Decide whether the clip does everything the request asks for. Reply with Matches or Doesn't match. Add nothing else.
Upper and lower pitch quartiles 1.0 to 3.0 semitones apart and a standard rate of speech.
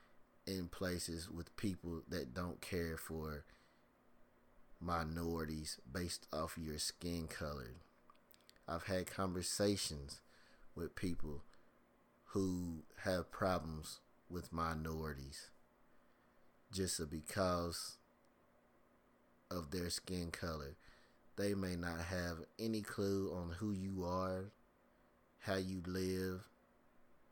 Doesn't match